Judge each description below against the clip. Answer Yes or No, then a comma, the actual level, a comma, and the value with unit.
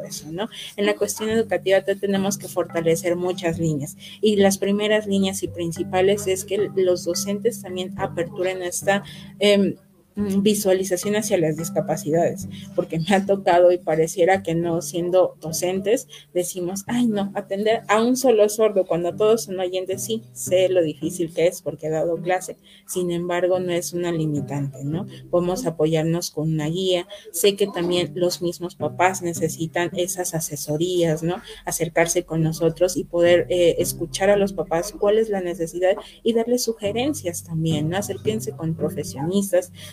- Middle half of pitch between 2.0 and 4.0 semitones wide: Yes, average, 2.9 semitones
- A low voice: No, medium, 180 Hz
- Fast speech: No, average, 160 wpm